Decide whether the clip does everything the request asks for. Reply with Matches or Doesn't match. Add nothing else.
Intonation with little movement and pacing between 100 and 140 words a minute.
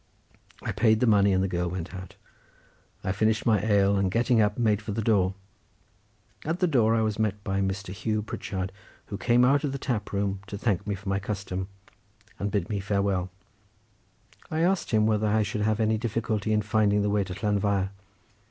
Doesn't match